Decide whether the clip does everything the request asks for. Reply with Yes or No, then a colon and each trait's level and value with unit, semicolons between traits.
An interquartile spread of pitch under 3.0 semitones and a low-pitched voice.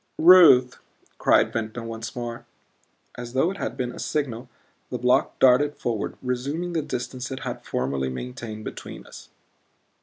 Yes: narrow, 2.6 semitones; low, 125 Hz